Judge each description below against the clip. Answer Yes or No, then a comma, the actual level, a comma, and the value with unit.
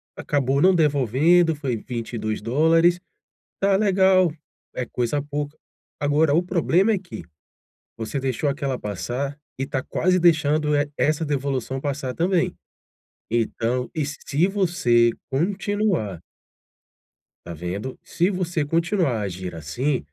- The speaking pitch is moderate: Yes, medium, 145 Hz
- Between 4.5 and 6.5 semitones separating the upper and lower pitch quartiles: Yes, wide, 5.5 semitones